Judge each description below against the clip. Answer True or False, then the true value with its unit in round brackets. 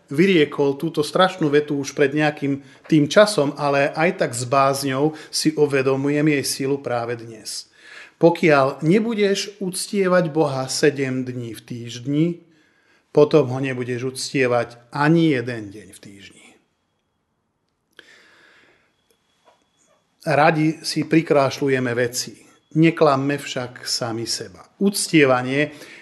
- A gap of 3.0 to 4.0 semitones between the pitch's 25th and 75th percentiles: True (3.5 semitones)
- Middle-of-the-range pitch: True (145 Hz)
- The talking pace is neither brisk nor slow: False (105 wpm)